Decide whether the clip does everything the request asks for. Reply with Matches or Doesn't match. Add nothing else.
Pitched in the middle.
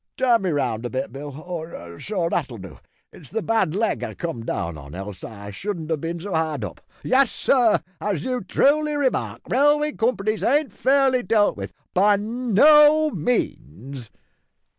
Doesn't match